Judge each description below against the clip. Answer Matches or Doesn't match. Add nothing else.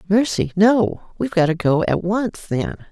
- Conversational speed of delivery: Matches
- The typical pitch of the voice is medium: Doesn't match